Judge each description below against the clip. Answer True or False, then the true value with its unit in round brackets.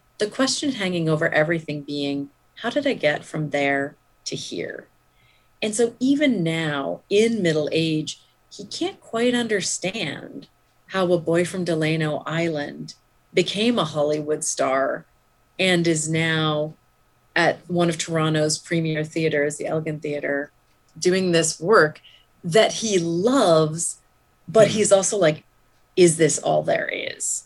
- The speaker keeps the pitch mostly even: False (4.1 semitones)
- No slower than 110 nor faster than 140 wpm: True (135 wpm)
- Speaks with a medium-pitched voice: True (165 Hz)